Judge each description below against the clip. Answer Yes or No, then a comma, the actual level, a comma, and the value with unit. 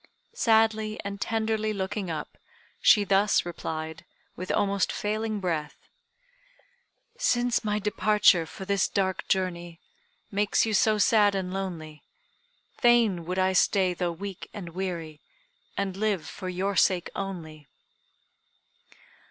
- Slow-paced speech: Yes, slow, 120 wpm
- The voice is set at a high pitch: Yes, high, 195 Hz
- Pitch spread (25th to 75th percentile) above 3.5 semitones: No, average, 3.1 semitones